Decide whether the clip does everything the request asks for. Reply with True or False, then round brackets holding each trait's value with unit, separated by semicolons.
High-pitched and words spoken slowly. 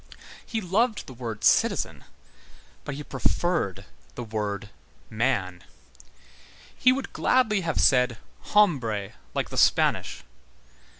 False (130 Hz; 110 wpm)